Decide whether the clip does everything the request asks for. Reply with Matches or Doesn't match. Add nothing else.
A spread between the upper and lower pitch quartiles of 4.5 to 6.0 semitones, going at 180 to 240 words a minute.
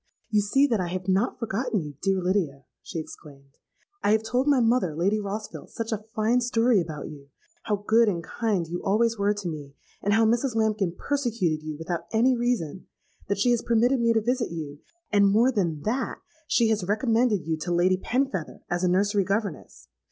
Matches